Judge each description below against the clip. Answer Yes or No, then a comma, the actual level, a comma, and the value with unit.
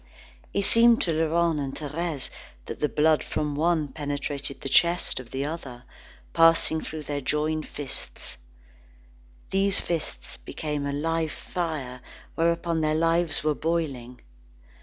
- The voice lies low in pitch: No, medium, 155 Hz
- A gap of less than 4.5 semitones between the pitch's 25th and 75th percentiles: Yes, average, 2.7 semitones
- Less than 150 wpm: Yes, slow, 135 wpm